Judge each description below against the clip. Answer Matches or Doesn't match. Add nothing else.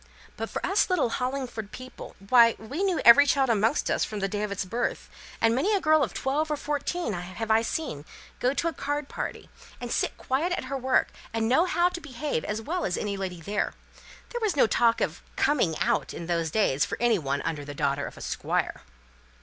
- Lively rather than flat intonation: Matches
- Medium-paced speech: Doesn't match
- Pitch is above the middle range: Matches